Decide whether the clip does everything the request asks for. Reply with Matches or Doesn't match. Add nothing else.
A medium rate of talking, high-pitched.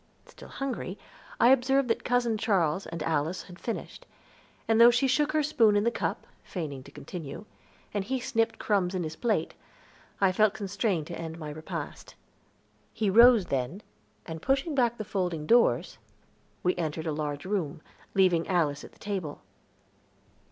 Matches